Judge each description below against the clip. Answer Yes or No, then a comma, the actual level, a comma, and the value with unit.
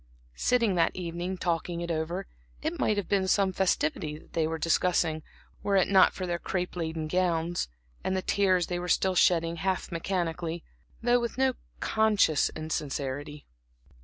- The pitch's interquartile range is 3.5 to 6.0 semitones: No, average, 2.7 semitones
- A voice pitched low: No, medium, 175 Hz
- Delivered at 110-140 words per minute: No, average, 165 wpm